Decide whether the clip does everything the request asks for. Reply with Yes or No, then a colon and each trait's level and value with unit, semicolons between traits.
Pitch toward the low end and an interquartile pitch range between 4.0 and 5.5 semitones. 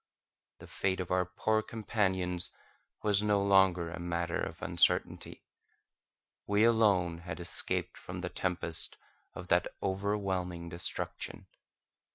No: very low, 95 Hz; narrow, 2.6 semitones